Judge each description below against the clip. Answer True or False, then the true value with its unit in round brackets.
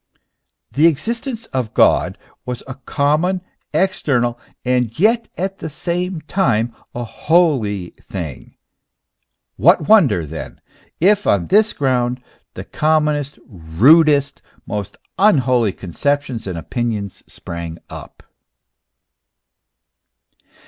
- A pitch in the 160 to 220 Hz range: False (135 Hz)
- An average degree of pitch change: False (7.1 semitones)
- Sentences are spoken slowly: True (100 wpm)